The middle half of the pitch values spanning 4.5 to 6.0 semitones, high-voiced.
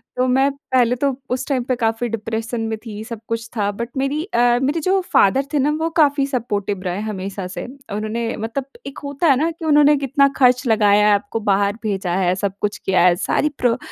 Yes: average, 4.8 semitones; high, 235 Hz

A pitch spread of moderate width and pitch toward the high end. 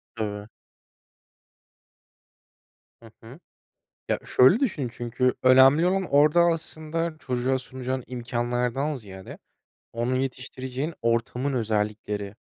No: average, 3.4 semitones; low, 130 Hz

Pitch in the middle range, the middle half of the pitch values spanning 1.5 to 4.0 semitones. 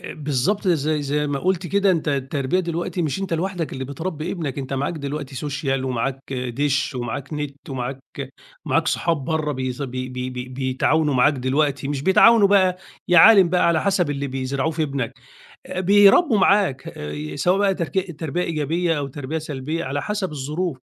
No: medium, 150 Hz; average, 4.7 semitones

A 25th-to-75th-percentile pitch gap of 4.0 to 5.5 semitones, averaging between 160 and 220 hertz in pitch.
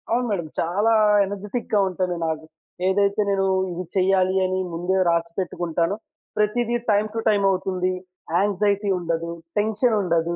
No: average, 2.9 semitones; high, 190 Hz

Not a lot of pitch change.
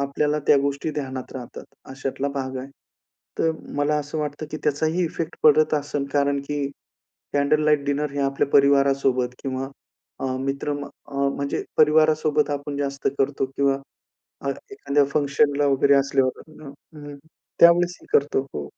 Yes: narrow, 1.4 semitones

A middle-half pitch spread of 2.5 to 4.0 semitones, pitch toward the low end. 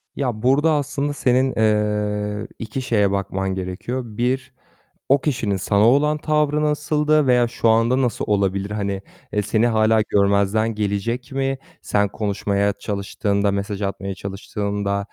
No: average, 4.4 semitones; low, 110 Hz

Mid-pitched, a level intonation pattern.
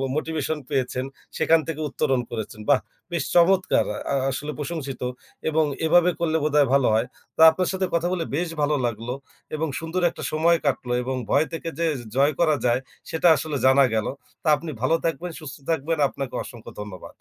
No: medium, 155 Hz; average, 3.8 semitones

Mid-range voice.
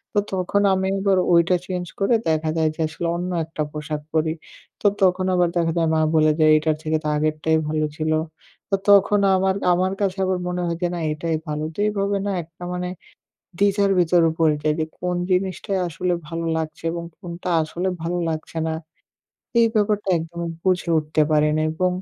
Yes: medium, 170 Hz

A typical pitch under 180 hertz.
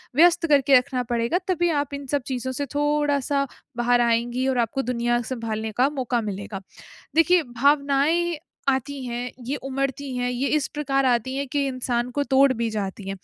No: very high, 265 Hz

